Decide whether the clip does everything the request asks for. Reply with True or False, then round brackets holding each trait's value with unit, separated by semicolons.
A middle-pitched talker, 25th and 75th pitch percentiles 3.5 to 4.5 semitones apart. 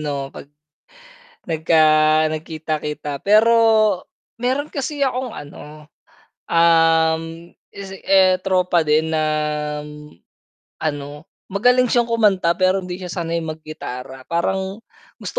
True (170 Hz; 4.2 semitones)